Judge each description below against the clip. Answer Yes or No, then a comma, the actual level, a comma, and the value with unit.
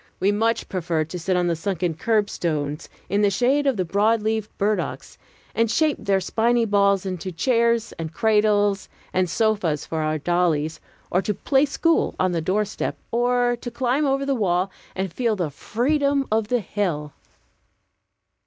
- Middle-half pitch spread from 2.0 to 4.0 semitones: No, average, 4.8 semitones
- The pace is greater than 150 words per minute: Yes, average, 170 wpm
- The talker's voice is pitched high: Yes, high, 205 Hz